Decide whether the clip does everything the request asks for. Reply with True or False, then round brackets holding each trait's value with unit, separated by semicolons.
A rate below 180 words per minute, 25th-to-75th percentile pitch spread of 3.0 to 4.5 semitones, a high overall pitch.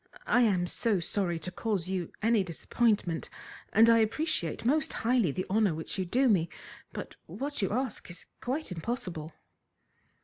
False (160 wpm; 5.2 semitones; 205 Hz)